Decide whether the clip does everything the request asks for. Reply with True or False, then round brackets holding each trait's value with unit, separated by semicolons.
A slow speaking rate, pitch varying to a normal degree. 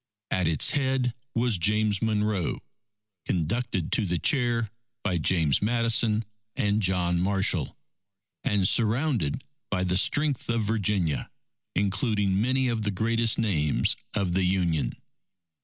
True (125 wpm; 4.1 semitones)